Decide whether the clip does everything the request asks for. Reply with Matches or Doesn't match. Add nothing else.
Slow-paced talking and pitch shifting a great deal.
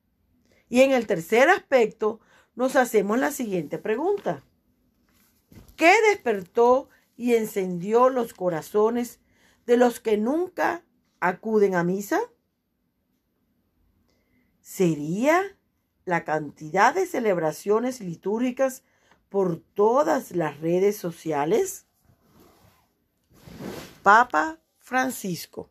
Matches